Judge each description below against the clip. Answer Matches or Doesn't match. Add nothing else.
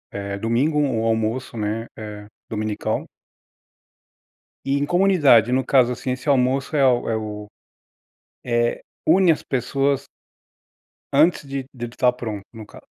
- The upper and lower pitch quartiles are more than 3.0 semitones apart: Matches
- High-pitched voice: Doesn't match